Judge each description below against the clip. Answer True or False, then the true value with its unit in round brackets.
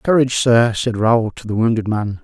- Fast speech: True (215 wpm)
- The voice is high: False (115 Hz)